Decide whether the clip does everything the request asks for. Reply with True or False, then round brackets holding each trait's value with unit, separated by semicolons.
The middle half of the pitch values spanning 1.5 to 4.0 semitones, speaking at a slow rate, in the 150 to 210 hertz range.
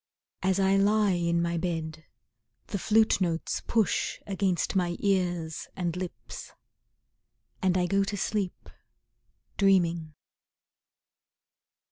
True (2.5 semitones; 105 wpm; 185 Hz)